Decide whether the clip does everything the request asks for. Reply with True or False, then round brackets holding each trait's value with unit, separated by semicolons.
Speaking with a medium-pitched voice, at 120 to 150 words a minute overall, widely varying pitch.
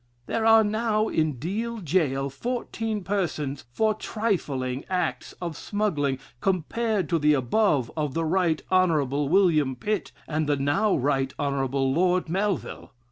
True (165 Hz; 135 wpm; 6.5 semitones)